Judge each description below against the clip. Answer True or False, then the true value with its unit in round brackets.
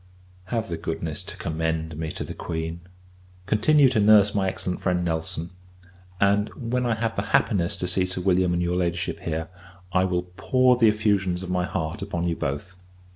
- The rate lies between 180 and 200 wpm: True (185 wpm)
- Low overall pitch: True (90 Hz)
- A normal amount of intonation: True (3.5 semitones)